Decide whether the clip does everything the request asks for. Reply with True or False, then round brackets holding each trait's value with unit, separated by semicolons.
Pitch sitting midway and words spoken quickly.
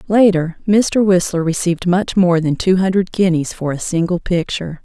False (180 Hz; 175 wpm)